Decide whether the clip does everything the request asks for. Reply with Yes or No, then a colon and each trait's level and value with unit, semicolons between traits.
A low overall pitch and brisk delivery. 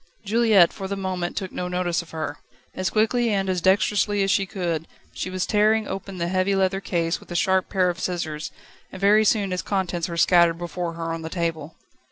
No: medium, 185 Hz; fast, 215 wpm